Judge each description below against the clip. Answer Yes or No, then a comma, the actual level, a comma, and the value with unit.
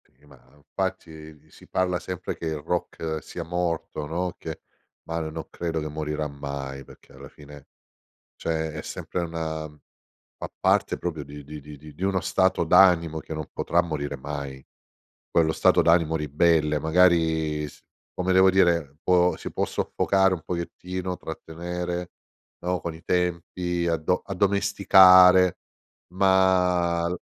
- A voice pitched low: Yes, very low, 85 Hz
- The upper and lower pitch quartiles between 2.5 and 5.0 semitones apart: Yes, average, 2.9 semitones